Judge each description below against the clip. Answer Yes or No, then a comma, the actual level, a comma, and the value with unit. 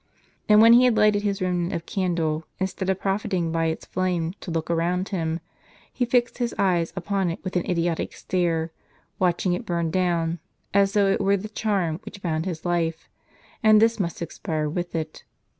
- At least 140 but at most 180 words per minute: No, average, 190 wpm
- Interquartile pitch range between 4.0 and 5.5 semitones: No, average, 3.1 semitones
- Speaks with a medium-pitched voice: Yes, medium, 180 Hz